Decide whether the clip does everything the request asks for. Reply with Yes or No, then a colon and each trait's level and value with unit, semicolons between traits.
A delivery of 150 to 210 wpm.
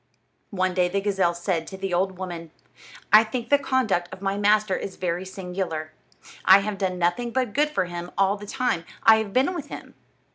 Yes: fast, 205 wpm